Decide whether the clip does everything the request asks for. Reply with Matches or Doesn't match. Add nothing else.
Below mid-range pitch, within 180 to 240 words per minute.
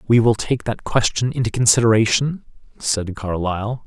Doesn't match